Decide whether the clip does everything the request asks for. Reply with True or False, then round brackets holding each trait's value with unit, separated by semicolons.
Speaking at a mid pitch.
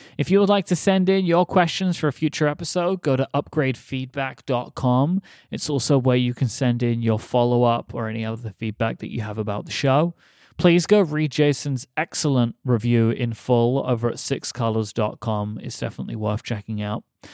False (130 Hz)